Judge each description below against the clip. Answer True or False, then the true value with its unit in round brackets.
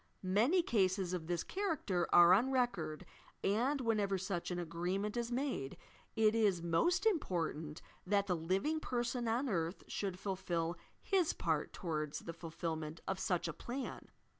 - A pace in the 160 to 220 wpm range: False (150 wpm)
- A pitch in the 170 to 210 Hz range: True (190 Hz)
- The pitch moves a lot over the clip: True (6.0 semitones)